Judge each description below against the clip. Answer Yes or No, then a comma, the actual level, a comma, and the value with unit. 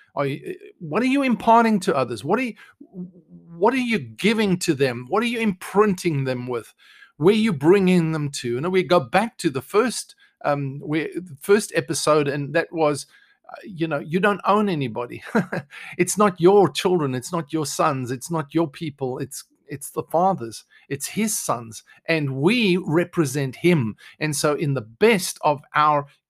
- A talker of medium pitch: Yes, medium, 170 Hz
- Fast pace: No, average, 185 wpm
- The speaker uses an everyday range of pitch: No, wide, 6.1 semitones